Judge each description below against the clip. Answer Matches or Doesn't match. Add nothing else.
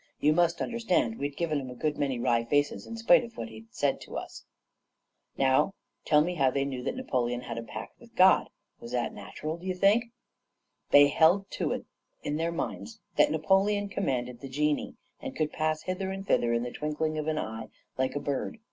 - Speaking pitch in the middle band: Matches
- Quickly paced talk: Matches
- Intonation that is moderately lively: Doesn't match